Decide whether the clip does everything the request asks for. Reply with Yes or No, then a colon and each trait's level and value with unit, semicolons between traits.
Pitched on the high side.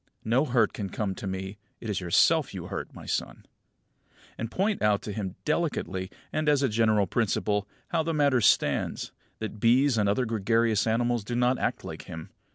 No: low, 115 Hz